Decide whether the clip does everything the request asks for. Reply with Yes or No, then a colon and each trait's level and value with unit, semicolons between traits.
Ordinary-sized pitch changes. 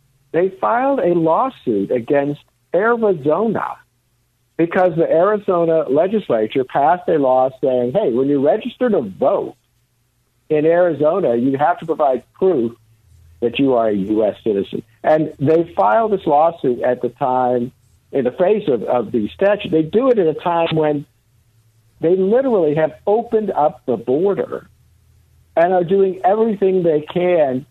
No: wide, 7.4 semitones